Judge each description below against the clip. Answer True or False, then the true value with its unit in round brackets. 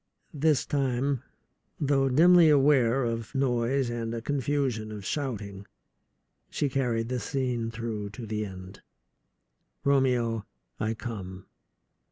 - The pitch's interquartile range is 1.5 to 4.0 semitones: True (3.7 semitones)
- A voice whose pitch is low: True (120 Hz)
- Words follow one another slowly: True (115 wpm)